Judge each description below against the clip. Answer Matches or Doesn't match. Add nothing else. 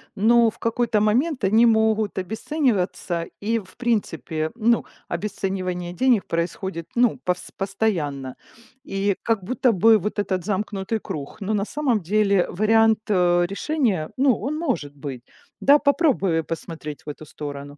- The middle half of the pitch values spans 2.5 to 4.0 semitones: Doesn't match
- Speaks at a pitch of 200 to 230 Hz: Matches